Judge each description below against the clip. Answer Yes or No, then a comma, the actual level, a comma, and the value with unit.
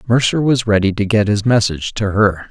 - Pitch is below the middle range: Yes, low, 105 Hz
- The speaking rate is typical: No, fast, 215 wpm